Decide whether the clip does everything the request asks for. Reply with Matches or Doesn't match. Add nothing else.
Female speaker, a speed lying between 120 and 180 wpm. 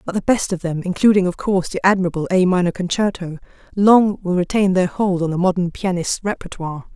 Doesn't match